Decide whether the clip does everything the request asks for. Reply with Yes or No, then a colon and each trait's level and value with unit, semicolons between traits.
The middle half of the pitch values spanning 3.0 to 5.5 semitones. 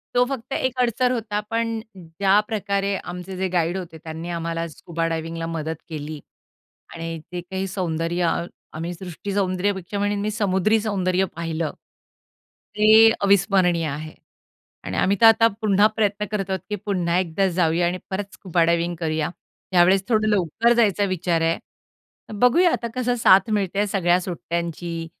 Yes: average, 3.6 semitones